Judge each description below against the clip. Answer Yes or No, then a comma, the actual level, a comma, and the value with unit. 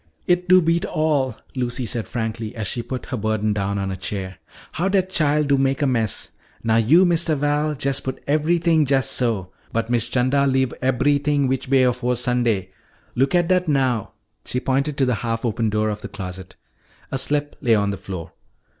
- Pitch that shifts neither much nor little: Yes, average, 4.6 semitones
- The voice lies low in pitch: Yes, low, 130 Hz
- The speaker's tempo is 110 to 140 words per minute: No, average, 190 wpm